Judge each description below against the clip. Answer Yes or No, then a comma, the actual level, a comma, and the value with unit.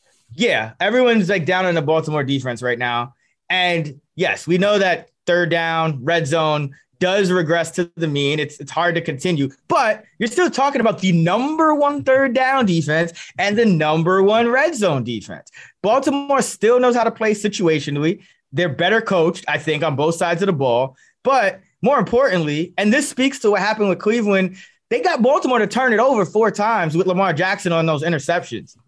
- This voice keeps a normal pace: Yes, average, 190 wpm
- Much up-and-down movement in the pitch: Yes, wide, 5.8 semitones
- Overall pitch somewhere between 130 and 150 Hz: No, medium, 185 Hz